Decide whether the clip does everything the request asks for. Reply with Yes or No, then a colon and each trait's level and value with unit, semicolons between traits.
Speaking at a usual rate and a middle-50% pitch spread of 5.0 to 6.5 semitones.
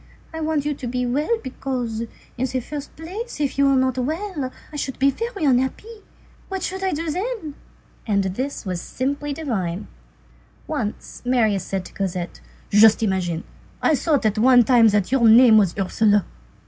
Yes: average, 175 wpm; wide, 5.5 semitones